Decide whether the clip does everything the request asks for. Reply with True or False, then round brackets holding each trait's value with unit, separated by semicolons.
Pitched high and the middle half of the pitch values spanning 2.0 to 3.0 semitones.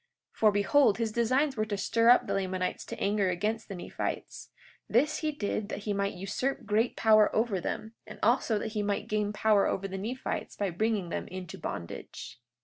True (210 Hz; 2.5 semitones)